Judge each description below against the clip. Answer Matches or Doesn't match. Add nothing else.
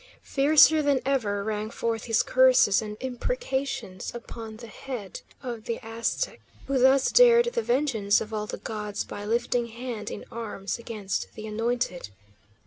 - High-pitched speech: Matches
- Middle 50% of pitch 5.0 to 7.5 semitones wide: Doesn't match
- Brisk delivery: Doesn't match